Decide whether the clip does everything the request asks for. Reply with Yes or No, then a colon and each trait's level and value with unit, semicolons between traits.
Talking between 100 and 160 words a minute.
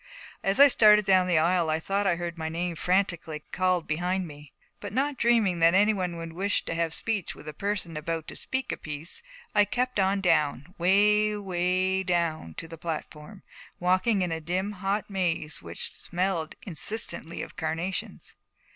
No: average, 180 wpm